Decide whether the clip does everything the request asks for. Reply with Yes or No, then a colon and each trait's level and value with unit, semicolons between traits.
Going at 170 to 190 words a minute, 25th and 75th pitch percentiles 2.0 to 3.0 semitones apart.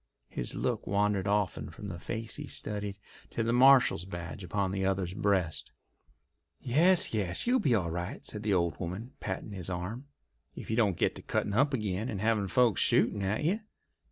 No: average, 185 wpm; average, 3.8 semitones